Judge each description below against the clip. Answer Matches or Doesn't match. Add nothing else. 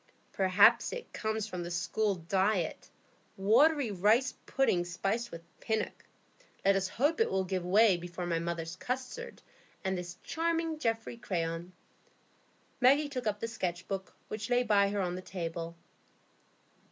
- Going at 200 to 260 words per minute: Doesn't match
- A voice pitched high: Matches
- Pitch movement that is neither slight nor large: Matches